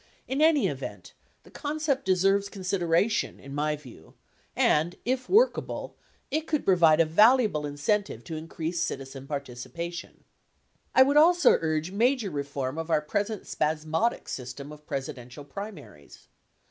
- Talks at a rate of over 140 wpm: No, slow, 135 wpm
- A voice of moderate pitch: Yes, medium, 170 Hz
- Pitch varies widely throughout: Yes, wide, 7.0 semitones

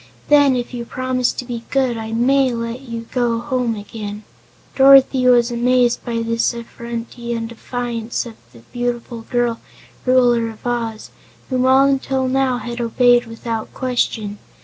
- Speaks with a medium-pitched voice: No, high, 240 Hz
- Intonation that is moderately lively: No, narrow, 1.7 semitones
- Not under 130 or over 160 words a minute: Yes, average, 150 wpm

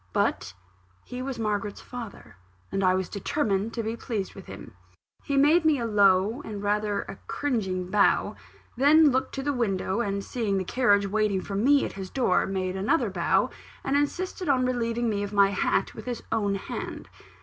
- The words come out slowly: No, average, 185 wpm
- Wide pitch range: No, average, 4.4 semitones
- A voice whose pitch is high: Yes, high, 215 Hz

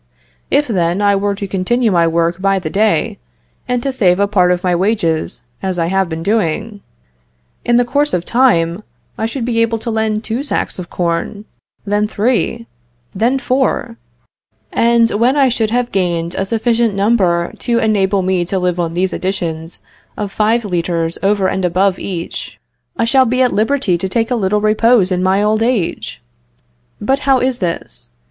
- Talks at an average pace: Yes, average, 180 wpm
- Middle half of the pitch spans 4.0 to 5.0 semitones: Yes, average, 4.4 semitones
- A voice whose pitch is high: Yes, high, 205 Hz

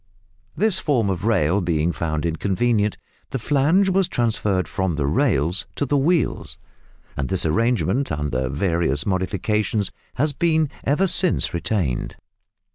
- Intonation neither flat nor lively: No, wide, 8.9 semitones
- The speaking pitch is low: Yes, low, 100 Hz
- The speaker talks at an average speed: No, slow, 130 wpm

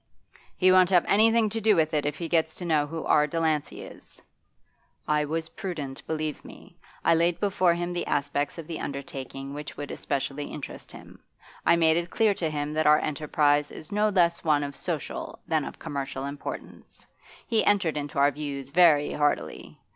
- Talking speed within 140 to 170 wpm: No, average, 185 wpm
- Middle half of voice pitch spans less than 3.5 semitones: Yes, average, 3.1 semitones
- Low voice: No, medium, 155 Hz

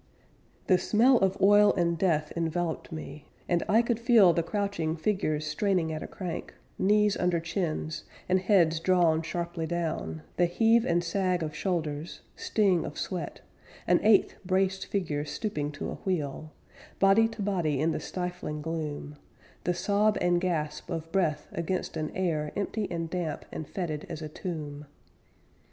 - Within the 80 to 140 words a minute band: No, average, 160 wpm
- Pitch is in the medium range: Yes, medium, 175 Hz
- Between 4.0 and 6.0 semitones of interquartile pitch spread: No, average, 3.6 semitones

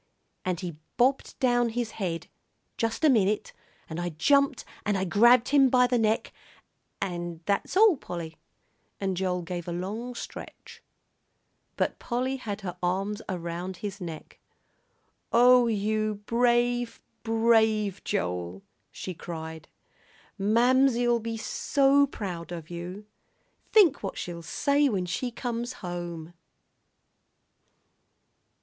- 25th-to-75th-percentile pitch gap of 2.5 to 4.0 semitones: No, wide, 5.6 semitones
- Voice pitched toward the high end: Yes, high, 210 Hz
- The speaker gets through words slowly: Yes, slow, 120 wpm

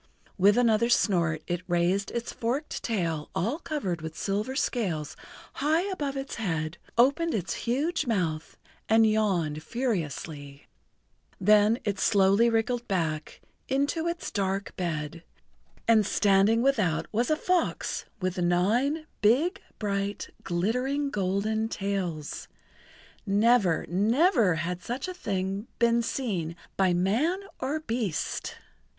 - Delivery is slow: Yes, slow, 120 wpm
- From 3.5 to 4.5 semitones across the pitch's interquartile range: No, wide, 5.6 semitones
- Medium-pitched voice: No, high, 210 Hz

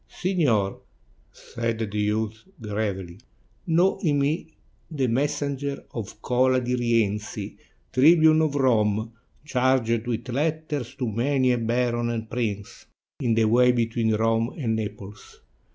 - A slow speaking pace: Yes, slow, 125 wpm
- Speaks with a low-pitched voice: Yes, low, 120 Hz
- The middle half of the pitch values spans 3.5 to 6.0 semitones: Yes, average, 3.8 semitones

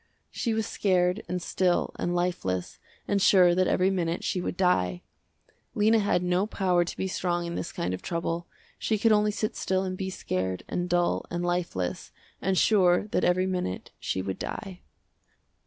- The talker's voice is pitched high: No, medium, 180 Hz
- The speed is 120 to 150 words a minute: No, average, 180 wpm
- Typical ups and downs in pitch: No, narrow, 1.7 semitones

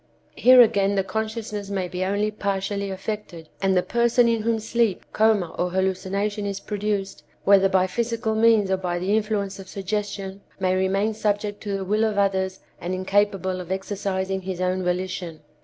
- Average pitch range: No, narrow, 2.1 semitones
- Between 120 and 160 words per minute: No, average, 175 wpm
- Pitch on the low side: No, high, 195 Hz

